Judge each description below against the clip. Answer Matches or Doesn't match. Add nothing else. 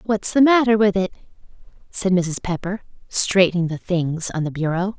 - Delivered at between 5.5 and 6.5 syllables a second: Doesn't match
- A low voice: Doesn't match